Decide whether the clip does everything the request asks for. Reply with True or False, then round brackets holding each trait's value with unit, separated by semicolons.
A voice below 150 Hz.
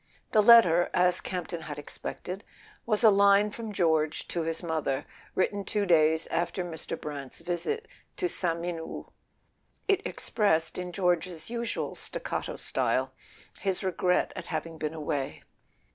False (175 Hz)